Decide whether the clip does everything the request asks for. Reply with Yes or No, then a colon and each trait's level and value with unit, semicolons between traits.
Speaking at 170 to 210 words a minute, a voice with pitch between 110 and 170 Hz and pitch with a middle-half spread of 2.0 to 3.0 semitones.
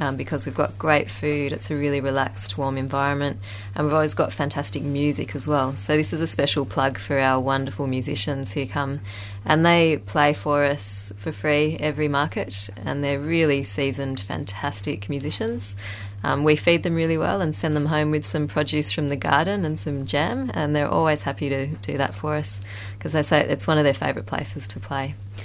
Yes: fast, 205 wpm; medium, 140 Hz; narrow, 2.4 semitones